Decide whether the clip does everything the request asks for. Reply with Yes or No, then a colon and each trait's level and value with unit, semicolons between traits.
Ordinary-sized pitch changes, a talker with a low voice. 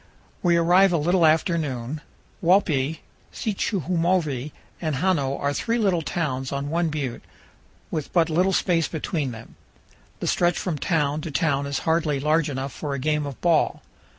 No: average, 3.6 semitones; medium, 155 Hz